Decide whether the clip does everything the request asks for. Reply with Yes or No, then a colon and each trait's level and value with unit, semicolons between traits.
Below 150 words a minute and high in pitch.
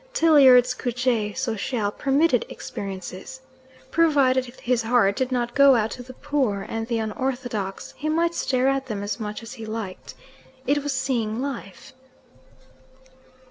Yes: average, 140 wpm; very high, 250 Hz